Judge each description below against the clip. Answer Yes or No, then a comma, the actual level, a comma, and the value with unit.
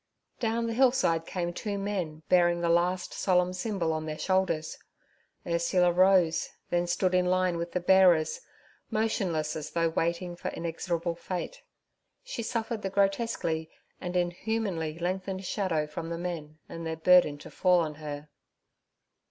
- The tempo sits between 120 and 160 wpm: Yes, average, 150 wpm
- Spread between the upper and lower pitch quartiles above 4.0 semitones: No, narrow, 2.5 semitones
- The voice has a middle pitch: Yes, medium, 175 Hz